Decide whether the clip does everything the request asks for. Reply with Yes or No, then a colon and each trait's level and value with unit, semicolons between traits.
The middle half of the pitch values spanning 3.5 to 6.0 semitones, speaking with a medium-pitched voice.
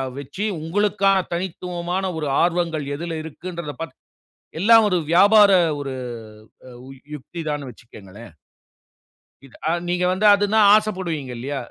Yes: average, 4.8 semitones; medium, 170 Hz